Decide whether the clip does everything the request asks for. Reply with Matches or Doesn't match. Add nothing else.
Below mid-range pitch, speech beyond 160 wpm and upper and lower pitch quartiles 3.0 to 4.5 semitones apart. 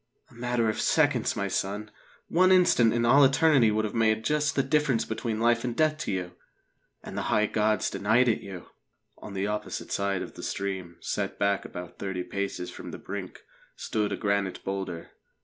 Matches